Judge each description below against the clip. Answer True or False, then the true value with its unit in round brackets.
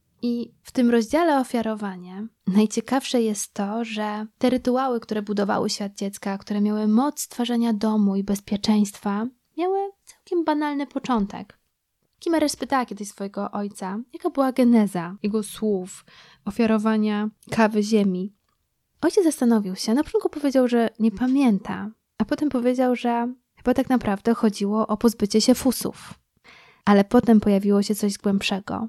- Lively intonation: False (3.6 semitones)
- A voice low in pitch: False (220 Hz)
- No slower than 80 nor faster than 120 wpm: False (135 wpm)